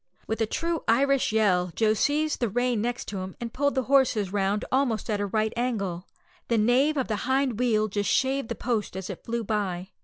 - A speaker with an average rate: No, fast, 210 wpm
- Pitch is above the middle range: Yes, high, 225 Hz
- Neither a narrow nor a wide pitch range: Yes, average, 3.9 semitones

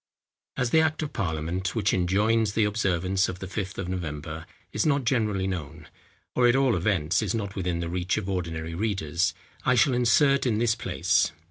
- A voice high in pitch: No, very low, 95 Hz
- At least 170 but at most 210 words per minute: Yes, average, 190 wpm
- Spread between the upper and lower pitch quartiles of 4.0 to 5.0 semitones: Yes, average, 4.7 semitones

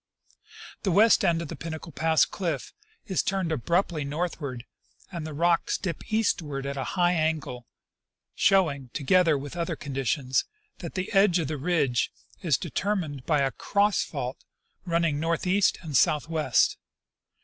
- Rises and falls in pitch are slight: No, average, 4.1 semitones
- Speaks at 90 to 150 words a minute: Yes, average, 145 wpm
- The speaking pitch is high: No, medium, 160 Hz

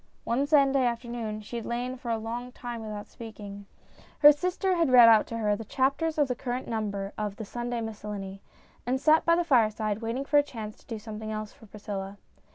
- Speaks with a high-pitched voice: Yes, high, 230 Hz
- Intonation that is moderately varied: Yes, average, 3.5 semitones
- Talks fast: Yes, fast, 215 wpm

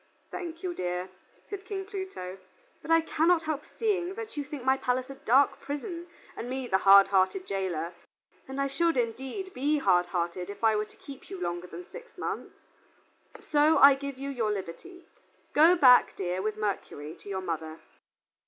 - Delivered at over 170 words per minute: Yes, average, 180 wpm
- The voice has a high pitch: Yes, very high, 265 Hz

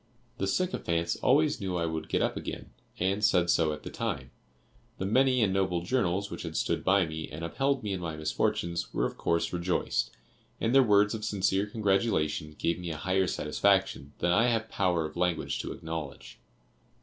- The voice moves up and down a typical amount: Yes, average, 3.8 semitones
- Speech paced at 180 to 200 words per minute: Yes, average, 190 wpm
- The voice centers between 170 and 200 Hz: No, very low, 95 Hz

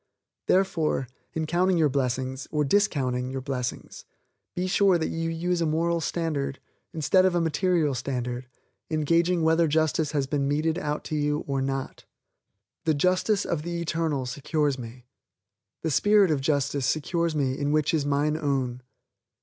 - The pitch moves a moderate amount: Yes, average, 3.4 semitones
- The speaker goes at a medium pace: Yes, average, 160 wpm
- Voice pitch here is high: No, medium, 155 Hz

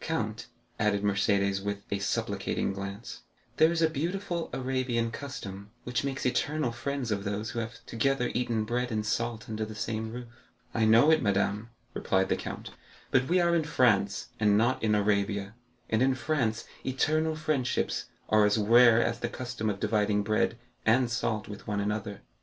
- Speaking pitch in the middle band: No, low, 115 Hz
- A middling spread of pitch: Yes, average, 3.9 semitones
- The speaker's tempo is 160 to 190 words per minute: Yes, average, 175 wpm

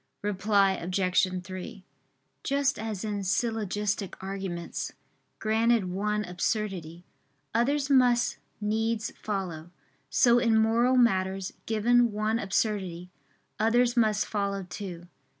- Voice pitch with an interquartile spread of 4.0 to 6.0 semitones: No, average, 3.3 semitones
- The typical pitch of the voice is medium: No, high, 210 Hz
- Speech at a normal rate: No, slow, 100 wpm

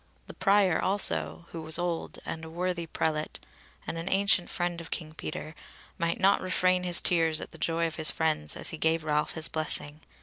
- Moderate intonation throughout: No, narrow, 2.2 semitones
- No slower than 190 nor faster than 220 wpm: Yes, average, 200 wpm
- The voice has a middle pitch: Yes, medium, 165 Hz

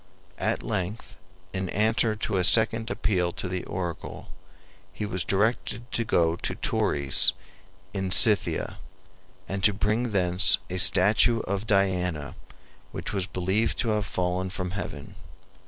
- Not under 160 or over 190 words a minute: No, average, 140 wpm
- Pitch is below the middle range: Yes, very low, 95 Hz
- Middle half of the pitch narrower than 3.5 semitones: Yes, average, 3.0 semitones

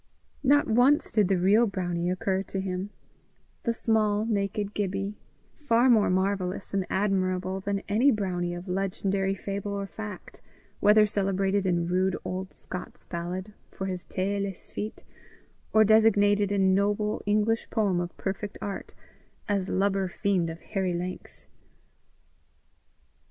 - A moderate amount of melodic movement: No, narrow, 2.0 semitones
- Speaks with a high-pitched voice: Yes, high, 195 Hz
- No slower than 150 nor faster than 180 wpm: No, slow, 135 wpm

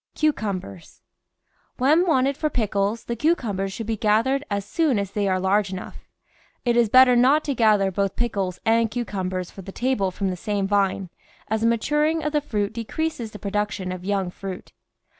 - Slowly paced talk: No, average, 185 wpm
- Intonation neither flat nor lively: Yes, average, 4.4 semitones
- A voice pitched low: No, high, 210 Hz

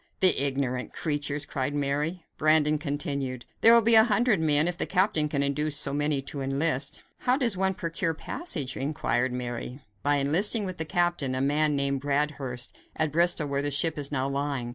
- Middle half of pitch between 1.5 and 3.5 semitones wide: Yes, average, 3.2 semitones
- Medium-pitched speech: Yes, medium, 145 Hz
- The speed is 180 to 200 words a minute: Yes, average, 185 wpm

